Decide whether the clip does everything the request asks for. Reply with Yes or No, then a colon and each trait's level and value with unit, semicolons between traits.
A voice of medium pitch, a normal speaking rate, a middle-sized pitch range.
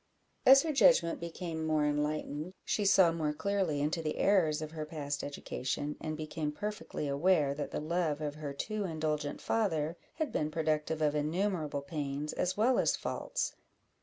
Yes: medium, 155 Hz; average, 165 wpm; average, 3.4 semitones